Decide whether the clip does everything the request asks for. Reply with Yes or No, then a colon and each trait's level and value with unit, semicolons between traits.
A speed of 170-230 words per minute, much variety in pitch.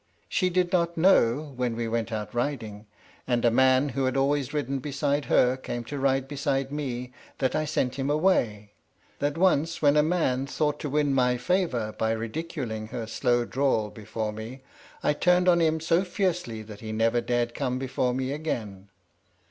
No: average, 180 wpm; average, 4.2 semitones